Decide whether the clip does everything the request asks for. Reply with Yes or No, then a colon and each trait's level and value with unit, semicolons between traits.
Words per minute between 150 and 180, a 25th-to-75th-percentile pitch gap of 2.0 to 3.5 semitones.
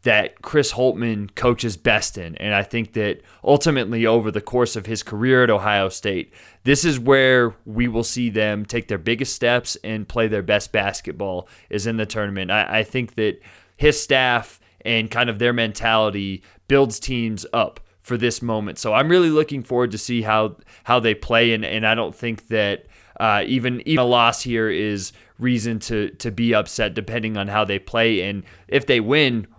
No: average, 195 wpm; narrow, 2.5 semitones